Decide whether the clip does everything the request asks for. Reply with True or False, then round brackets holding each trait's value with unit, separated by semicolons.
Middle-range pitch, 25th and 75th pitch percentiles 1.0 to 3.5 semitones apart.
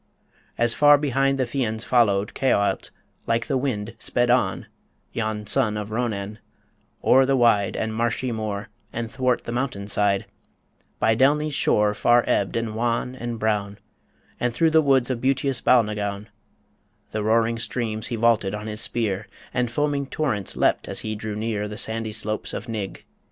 False (115 Hz; 3.1 semitones)